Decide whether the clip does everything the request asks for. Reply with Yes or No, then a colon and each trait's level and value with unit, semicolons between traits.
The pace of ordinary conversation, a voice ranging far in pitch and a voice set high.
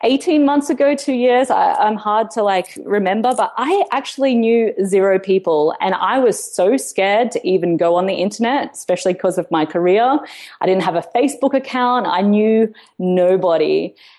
Yes: average, 180 wpm; wide, 5.9 semitones; high, 215 Hz